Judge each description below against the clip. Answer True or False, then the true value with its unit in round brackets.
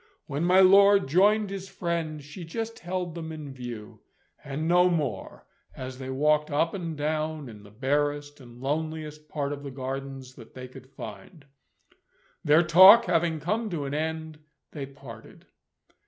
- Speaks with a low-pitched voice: False (150 Hz)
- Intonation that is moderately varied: True (3.9 semitones)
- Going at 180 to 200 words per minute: False (160 wpm)